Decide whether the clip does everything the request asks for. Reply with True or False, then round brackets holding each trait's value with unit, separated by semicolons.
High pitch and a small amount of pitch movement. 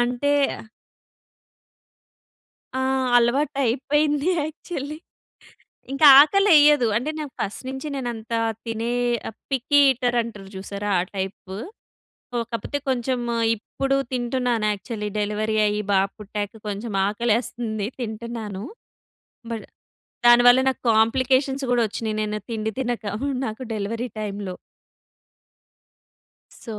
False (235 Hz; 3.7 semitones)